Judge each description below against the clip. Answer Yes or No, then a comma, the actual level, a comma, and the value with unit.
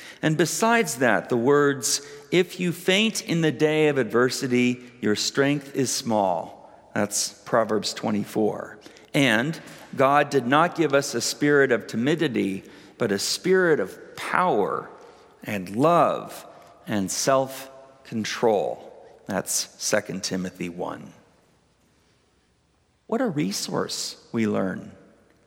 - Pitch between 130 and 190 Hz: Yes, low, 135 Hz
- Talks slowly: Yes, slow, 115 wpm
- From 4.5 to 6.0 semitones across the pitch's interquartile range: Yes, average, 5.1 semitones